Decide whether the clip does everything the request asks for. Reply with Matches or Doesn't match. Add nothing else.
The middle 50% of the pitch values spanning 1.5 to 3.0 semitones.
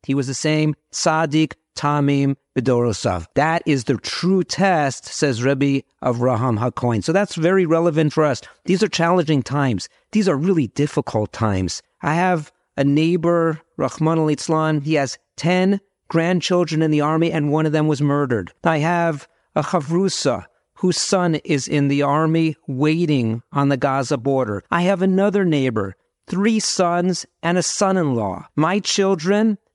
Doesn't match